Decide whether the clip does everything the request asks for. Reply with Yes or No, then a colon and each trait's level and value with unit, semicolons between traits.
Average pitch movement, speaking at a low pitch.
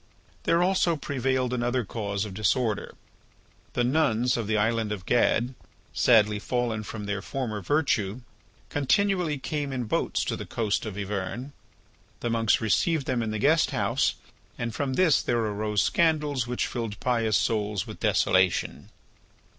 Yes: average, 4.1 semitones; low, 120 Hz